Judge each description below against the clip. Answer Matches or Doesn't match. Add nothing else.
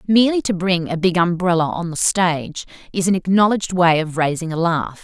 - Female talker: Matches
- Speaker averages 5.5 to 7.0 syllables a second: Matches